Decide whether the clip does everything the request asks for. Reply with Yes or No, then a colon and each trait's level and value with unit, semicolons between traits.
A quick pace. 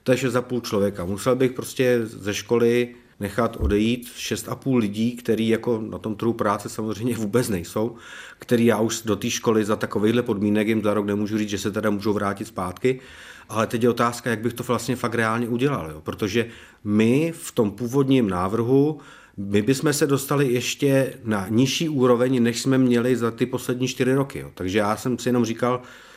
Yes: fast, 190 wpm